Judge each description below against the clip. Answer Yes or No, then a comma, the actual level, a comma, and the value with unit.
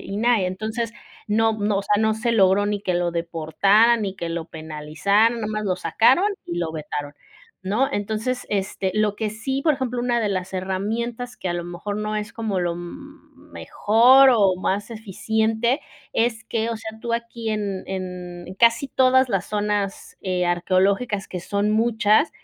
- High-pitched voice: Yes, high, 210 Hz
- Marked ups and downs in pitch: No, average, 3.6 semitones